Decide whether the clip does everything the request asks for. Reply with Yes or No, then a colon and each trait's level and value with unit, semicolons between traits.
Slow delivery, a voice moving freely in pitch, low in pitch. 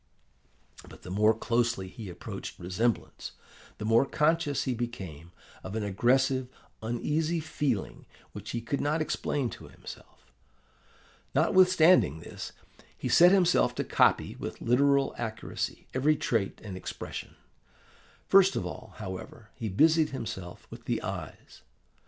Yes: slow, 130 wpm; wide, 6.2 semitones; low, 120 Hz